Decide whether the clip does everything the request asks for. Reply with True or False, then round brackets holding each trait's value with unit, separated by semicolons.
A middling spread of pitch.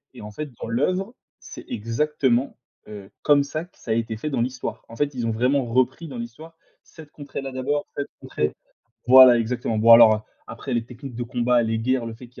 True (3.5 semitones)